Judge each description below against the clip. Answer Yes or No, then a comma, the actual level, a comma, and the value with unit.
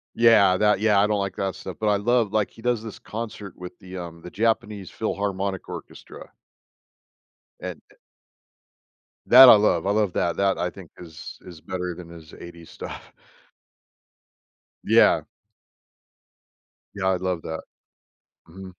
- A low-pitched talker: Yes, very low, 95 Hz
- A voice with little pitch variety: No, average, 3.0 semitones